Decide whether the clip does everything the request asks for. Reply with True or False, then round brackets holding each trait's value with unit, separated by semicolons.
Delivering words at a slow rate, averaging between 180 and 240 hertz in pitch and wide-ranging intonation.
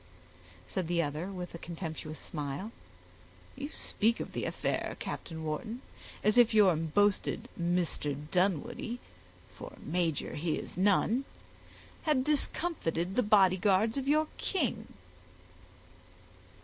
True (115 wpm; 190 Hz; 5.9 semitones)